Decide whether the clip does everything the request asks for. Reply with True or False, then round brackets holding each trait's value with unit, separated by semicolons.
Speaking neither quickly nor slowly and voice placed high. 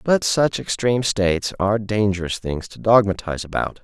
False (155 wpm; 105 Hz)